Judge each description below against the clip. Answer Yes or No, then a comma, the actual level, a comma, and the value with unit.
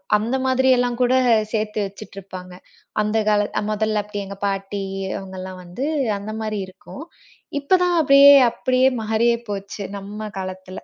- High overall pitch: Yes, high, 210 Hz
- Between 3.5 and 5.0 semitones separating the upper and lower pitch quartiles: Yes, average, 3.8 semitones